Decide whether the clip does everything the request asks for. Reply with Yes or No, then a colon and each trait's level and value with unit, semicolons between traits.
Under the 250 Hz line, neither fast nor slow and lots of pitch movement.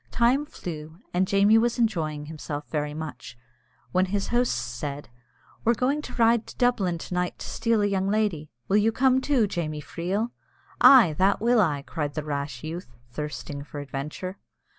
Yes: medium, 185 Hz; average, 175 wpm; wide, 7.0 semitones